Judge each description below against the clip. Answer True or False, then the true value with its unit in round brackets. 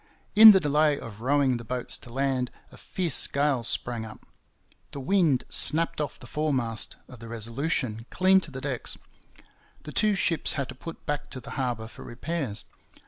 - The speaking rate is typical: True (180 wpm)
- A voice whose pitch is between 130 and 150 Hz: True (135 Hz)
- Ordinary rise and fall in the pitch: True (4.4 semitones)